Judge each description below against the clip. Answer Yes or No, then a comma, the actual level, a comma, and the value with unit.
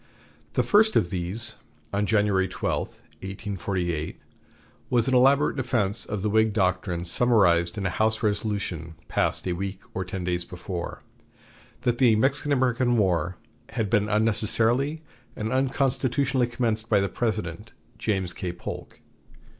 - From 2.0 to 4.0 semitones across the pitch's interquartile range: No, average, 4.6 semitones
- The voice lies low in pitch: Yes, low, 105 Hz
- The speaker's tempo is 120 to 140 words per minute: Yes, slow, 135 wpm